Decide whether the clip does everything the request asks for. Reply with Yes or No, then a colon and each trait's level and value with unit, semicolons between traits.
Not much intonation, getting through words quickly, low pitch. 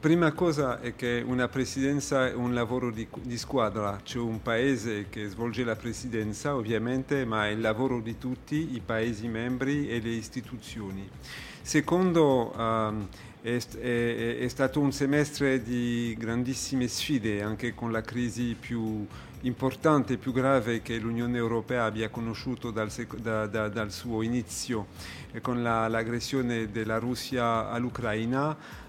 No: narrow, 2.3 semitones; average, 145 wpm; low, 120 Hz